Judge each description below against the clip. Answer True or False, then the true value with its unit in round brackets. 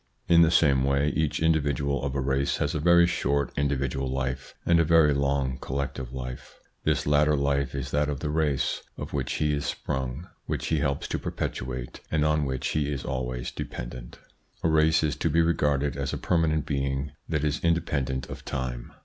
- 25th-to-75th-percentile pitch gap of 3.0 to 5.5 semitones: False (2.4 semitones)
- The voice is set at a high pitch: False (70 Hz)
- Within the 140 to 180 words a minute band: False (190 wpm)